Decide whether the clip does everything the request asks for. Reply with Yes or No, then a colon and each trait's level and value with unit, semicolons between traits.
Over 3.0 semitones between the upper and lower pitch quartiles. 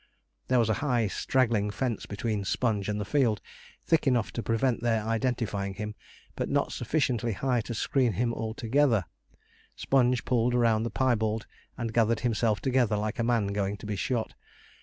No: narrow, 2.6 semitones